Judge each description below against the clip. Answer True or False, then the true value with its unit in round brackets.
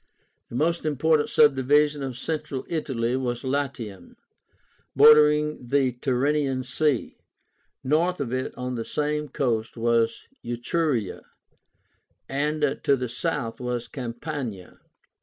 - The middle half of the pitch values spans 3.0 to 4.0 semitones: True (3.7 semitones)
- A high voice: False (135 Hz)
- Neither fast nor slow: False (115 wpm)